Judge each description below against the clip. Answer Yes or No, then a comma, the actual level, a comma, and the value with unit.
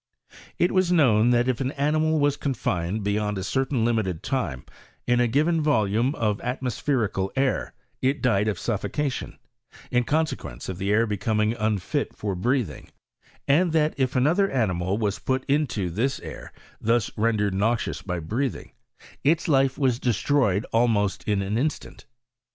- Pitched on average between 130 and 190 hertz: No, low, 120 Hz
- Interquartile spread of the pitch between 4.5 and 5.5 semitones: Yes, average, 5.0 semitones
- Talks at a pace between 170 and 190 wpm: No, average, 160 wpm